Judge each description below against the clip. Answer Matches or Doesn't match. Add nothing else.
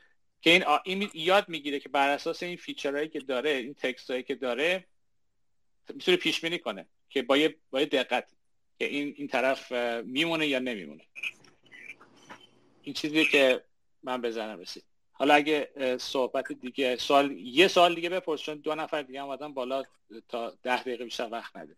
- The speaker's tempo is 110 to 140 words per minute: Doesn't match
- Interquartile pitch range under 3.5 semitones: Doesn't match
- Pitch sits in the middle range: Matches